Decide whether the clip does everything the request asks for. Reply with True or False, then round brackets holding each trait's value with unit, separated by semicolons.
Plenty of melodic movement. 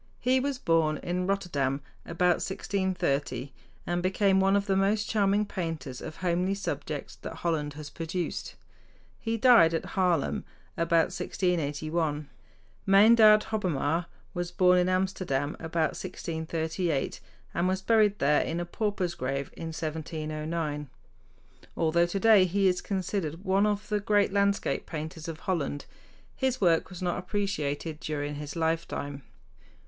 False (3.8 semitones)